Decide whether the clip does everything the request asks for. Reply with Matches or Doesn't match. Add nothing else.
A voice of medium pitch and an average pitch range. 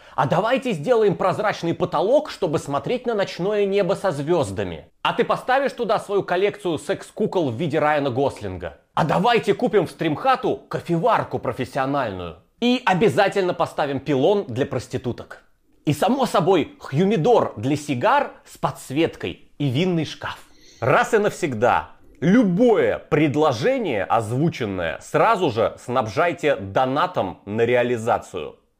Doesn't match